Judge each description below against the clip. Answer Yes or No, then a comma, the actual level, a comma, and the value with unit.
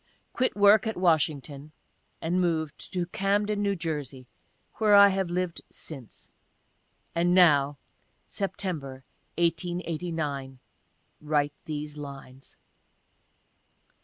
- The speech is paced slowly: Yes, slow, 100 wpm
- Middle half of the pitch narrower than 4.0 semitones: No, average, 4.3 semitones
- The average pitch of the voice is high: No, medium, 165 Hz